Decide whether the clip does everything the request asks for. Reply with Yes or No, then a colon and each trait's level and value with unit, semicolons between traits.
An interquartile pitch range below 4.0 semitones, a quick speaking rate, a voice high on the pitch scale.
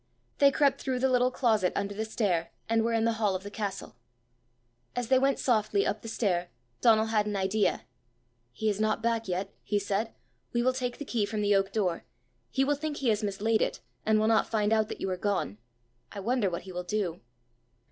Yes: average, 2.9 semitones; fast, 220 wpm; high, 215 Hz